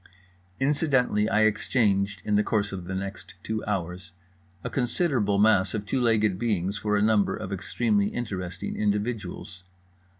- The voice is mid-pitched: No, low, 105 Hz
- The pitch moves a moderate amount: No, narrow, 2.3 semitones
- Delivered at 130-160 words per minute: Yes, average, 145 wpm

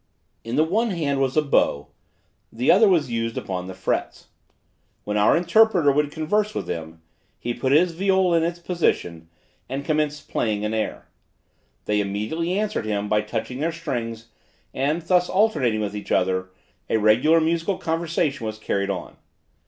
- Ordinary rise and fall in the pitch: No, wide, 7.9 semitones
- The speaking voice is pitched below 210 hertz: Yes, medium, 140 Hz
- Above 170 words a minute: No, average, 165 wpm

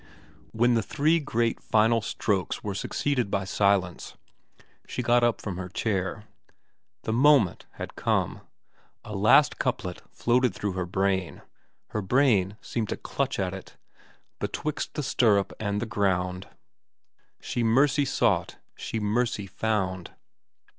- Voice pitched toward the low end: Yes, low, 105 Hz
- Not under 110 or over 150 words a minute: Yes, slow, 135 wpm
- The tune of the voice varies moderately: Yes, average, 4.1 semitones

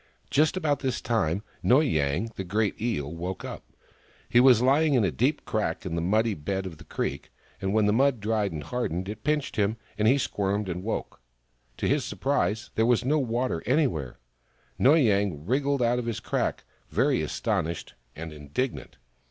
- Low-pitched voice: Yes, low, 110 Hz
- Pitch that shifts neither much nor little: No, wide, 5.9 semitones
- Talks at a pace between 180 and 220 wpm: Yes, average, 185 wpm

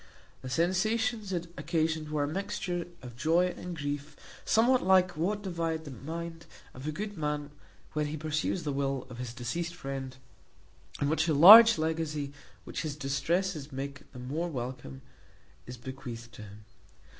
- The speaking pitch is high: No, medium, 155 Hz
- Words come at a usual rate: Yes, average, 160 wpm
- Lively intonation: No, average, 4.2 semitones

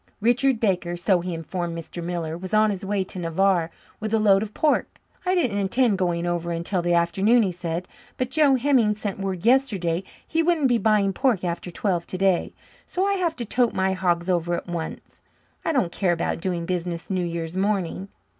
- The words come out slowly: No, average, 200 wpm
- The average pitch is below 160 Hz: No, high, 190 Hz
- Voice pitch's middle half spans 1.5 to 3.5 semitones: No, average, 4.3 semitones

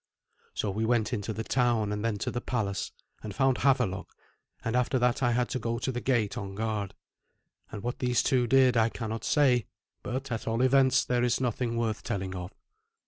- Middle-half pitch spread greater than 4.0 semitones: No, narrow, 2.5 semitones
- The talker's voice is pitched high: No, low, 120 Hz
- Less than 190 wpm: No, average, 200 wpm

